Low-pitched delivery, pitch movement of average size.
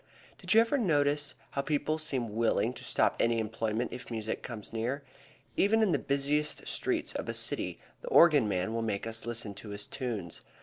Yes: low, 120 Hz; average, 4.9 semitones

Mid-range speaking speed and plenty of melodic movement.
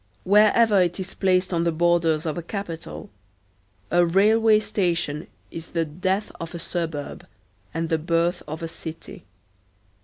No: average, 150 wpm; narrow, 2.6 semitones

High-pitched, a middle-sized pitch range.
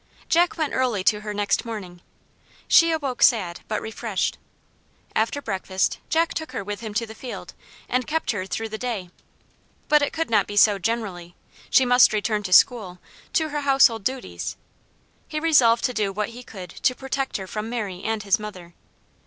Yes: high, 225 Hz; average, 4.3 semitones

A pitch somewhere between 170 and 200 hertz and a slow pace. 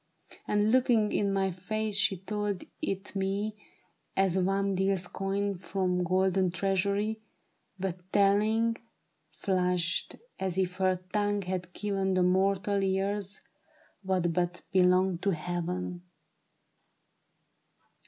Yes: high, 190 Hz; slow, 110 wpm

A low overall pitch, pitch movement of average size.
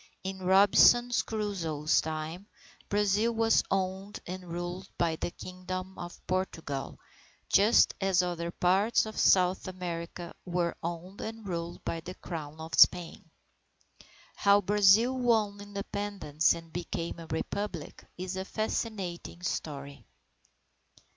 No: medium, 185 Hz; average, 3.1 semitones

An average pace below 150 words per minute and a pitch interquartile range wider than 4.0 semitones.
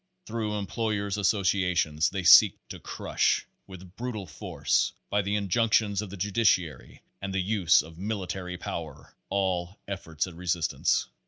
No: average, 140 wpm; average, 2.7 semitones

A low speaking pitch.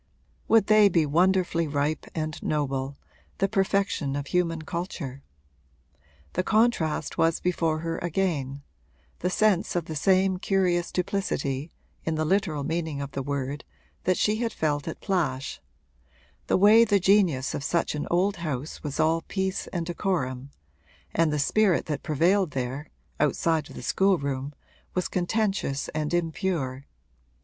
No: medium, 165 Hz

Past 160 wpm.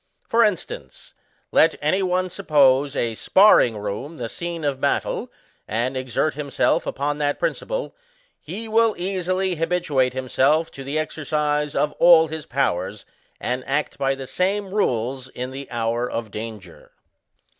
No: average, 150 wpm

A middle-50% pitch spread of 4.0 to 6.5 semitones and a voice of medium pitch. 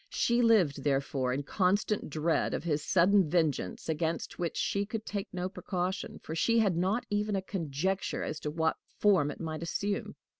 Yes: average, 4.6 semitones; medium, 175 Hz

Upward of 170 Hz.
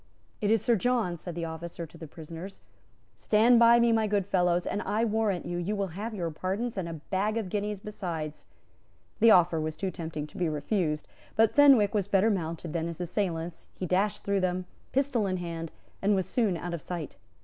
Yes: medium, 185 Hz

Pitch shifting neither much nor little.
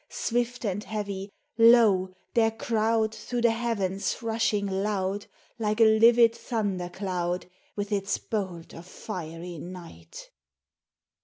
Yes: average, 3.4 semitones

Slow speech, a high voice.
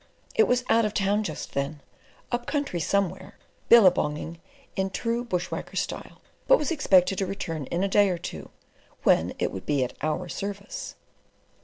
No: average, 170 wpm; high, 195 Hz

